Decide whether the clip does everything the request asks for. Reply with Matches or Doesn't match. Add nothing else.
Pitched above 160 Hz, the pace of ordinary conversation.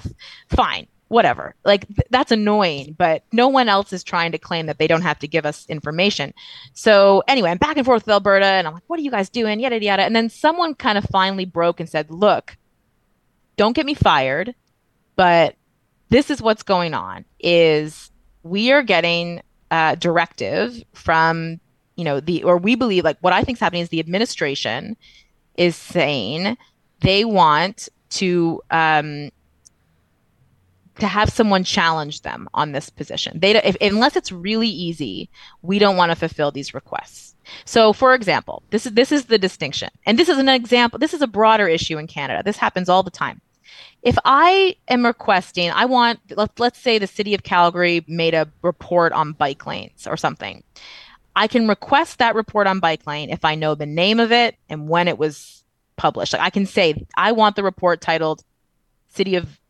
Matches